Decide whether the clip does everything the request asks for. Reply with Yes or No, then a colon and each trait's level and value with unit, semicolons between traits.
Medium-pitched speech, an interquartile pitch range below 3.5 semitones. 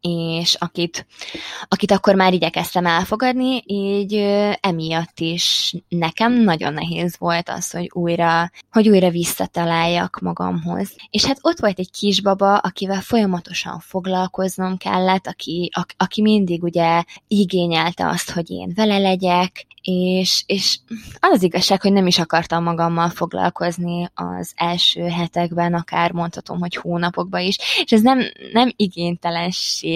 Yes: medium, 180 Hz; narrow, 2.6 semitones